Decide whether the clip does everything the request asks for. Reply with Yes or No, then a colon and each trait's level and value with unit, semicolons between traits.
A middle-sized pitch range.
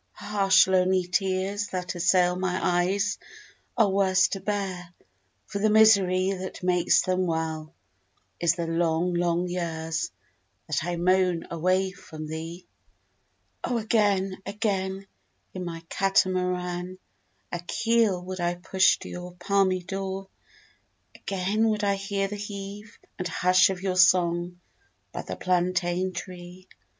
No: narrow, 1.8 semitones